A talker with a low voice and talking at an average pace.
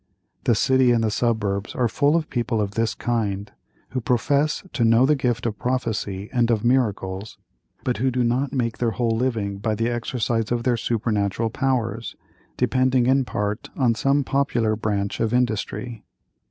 Yes: low, 115 Hz; average, 170 wpm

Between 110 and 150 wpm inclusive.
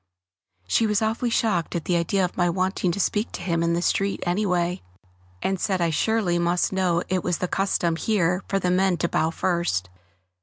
No: average, 200 wpm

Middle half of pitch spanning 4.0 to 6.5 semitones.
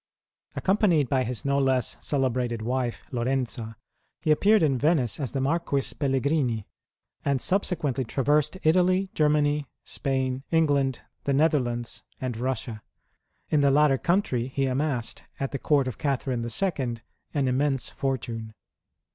No: average, 3.1 semitones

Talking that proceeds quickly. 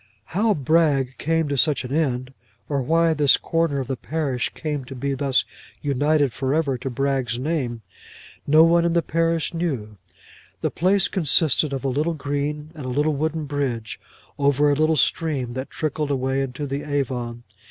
No: average, 175 wpm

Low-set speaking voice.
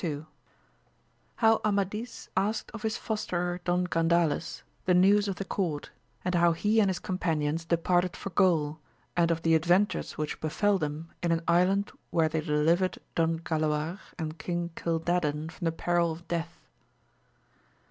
No: medium, 170 Hz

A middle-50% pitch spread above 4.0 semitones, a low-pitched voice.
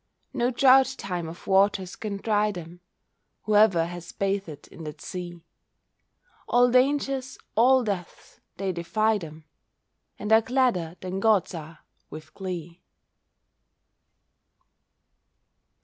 No: average, 4.6 semitones; high, 195 Hz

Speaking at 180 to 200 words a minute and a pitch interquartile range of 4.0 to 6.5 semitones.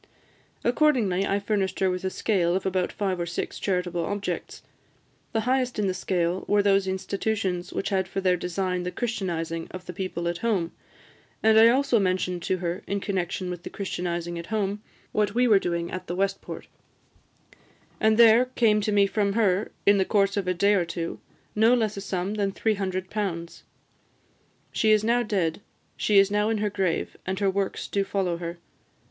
No: average, 190 wpm; average, 2.7 semitones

